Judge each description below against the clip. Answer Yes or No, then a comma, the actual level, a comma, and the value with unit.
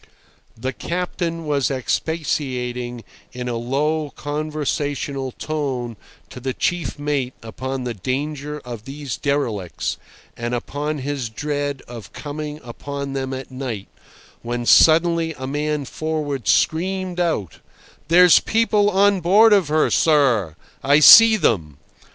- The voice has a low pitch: No, medium, 145 Hz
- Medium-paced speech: No, slow, 125 wpm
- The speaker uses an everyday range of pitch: Yes, average, 4.0 semitones